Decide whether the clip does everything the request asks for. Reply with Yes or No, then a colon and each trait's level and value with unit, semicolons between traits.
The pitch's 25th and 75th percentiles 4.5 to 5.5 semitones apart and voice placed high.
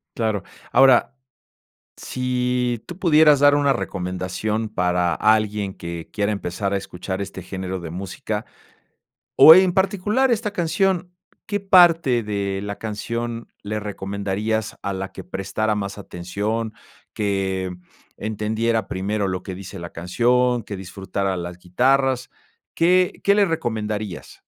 No: average, 5.0 semitones; low, 105 Hz